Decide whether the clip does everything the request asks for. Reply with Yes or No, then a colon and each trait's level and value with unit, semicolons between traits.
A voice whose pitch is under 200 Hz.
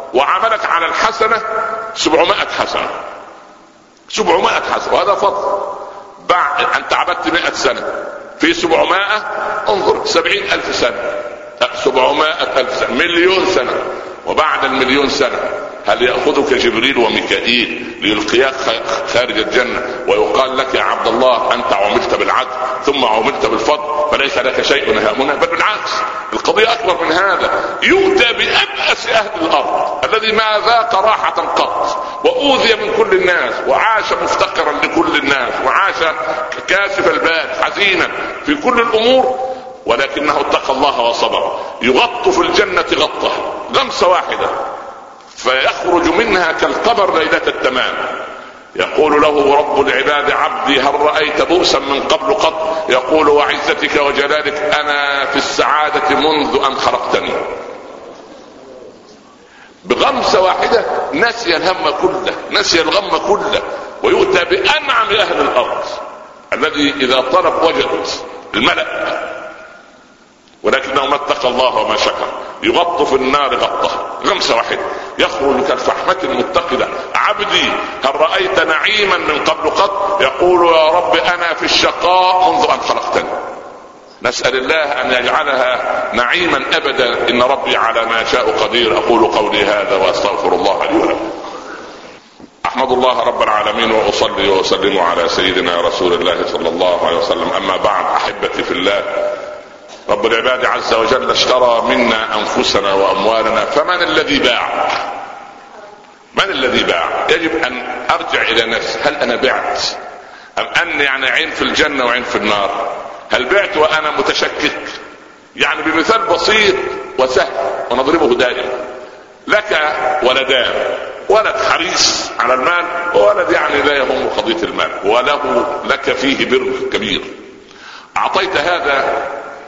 No: high, 220 Hz